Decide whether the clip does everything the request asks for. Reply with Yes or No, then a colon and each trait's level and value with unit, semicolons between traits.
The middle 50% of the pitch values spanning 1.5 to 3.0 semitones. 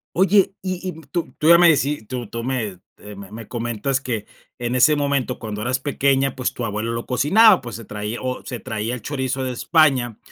No: average, 3.8 semitones